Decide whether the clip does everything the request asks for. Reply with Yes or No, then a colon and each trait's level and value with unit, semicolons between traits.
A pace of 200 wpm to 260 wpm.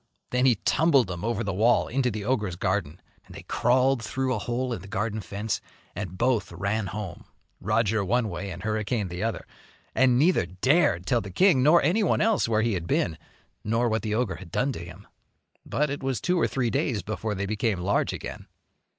Yes: fast, 205 wpm